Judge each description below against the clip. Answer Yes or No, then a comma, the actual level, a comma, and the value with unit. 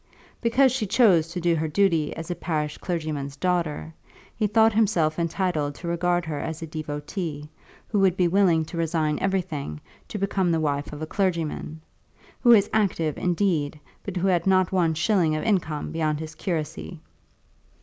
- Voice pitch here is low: No, medium, 170 Hz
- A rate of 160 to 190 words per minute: Yes, average, 170 wpm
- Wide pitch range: No, average, 3.6 semitones